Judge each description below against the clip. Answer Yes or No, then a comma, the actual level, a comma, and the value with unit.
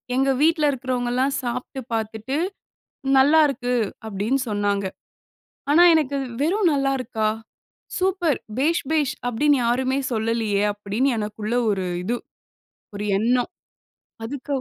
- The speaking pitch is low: No, very high, 255 Hz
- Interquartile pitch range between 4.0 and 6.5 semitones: Yes, average, 4.4 semitones